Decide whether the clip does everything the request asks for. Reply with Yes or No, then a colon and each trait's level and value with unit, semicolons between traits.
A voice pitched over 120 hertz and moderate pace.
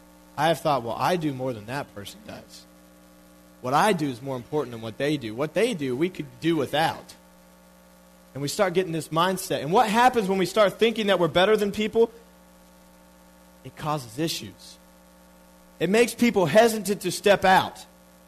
Yes: low, 135 Hz; average, 185 wpm